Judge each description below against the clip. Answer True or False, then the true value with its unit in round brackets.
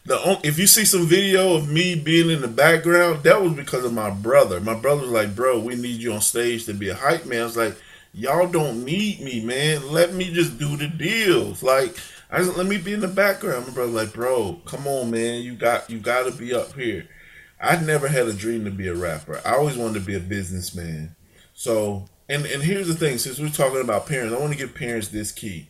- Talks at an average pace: False (250 wpm)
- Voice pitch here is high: False (130 Hz)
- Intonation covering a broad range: True (6.7 semitones)